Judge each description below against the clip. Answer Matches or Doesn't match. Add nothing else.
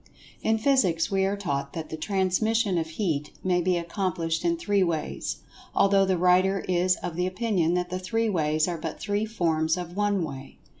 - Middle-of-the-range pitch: Matches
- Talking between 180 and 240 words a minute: Matches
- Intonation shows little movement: Doesn't match